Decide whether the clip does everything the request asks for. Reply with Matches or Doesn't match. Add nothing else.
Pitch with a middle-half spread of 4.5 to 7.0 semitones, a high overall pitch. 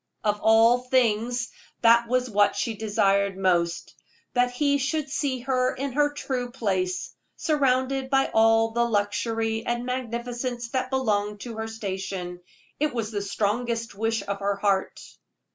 Doesn't match